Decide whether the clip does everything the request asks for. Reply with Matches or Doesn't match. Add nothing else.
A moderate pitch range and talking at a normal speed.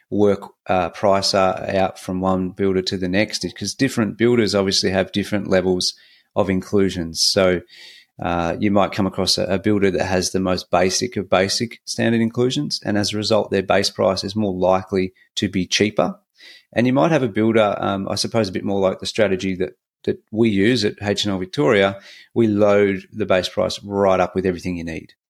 Doesn't match